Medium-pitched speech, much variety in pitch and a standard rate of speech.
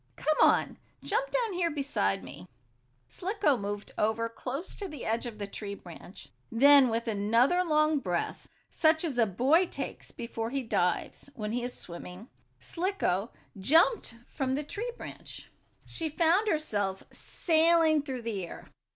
No: very high, 260 Hz; wide, 7.2 semitones; average, 155 wpm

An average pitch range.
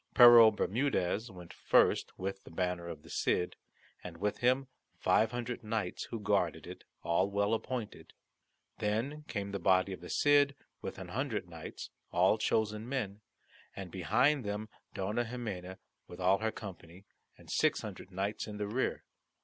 Yes: average, 4.1 semitones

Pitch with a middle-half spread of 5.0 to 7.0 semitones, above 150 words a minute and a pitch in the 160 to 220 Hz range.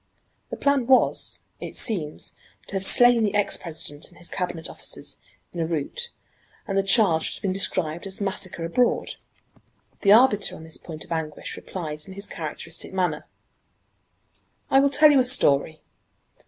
Yes: wide, 5.4 semitones; average, 170 wpm; high, 190 Hz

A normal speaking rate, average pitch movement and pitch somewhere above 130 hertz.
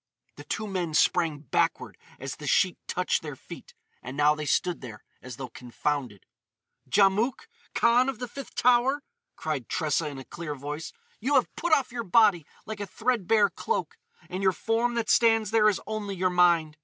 No: average, 180 wpm; wide, 7.4 semitones; high, 190 Hz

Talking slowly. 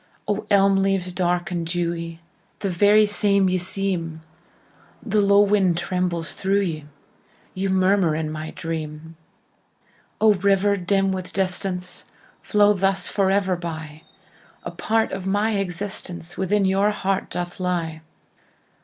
Yes: slow, 110 wpm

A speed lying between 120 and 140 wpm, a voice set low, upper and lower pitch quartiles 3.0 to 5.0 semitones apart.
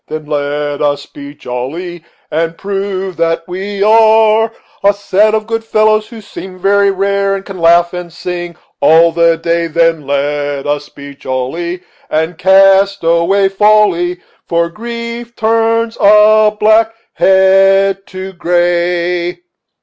No: slow, 135 wpm; medium, 185 Hz; average, 3.6 semitones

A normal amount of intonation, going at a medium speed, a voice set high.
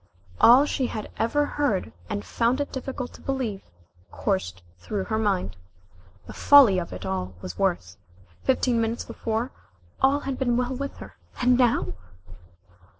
No: wide, 6.1 semitones; average, 150 wpm; high, 230 Hz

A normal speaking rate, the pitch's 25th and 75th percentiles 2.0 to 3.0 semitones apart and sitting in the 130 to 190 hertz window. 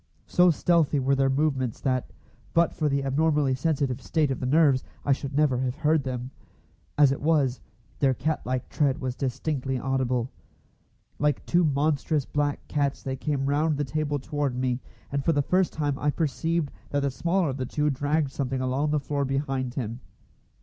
Yes: average, 185 wpm; narrow, 2.4 semitones; medium, 140 Hz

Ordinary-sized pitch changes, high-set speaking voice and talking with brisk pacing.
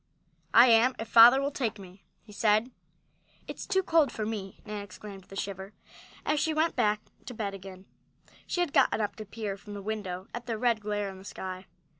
Yes: average, 3.4 semitones; high, 210 Hz; fast, 210 wpm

